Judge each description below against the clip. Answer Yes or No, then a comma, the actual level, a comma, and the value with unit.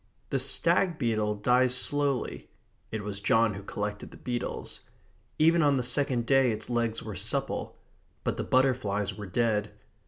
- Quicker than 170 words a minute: No, average, 155 wpm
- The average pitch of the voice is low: Yes, low, 120 Hz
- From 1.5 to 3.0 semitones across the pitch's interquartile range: No, average, 4.2 semitones